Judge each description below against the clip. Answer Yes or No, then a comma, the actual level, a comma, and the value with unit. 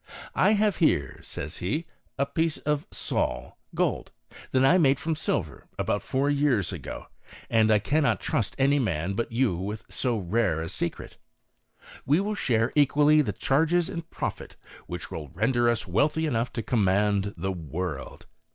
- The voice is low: Yes, low, 120 Hz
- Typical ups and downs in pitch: No, wide, 7.2 semitones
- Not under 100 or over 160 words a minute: No, average, 170 wpm